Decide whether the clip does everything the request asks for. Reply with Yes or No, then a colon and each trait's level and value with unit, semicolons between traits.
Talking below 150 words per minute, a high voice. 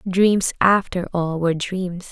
No: average, 140 wpm; medium, 180 Hz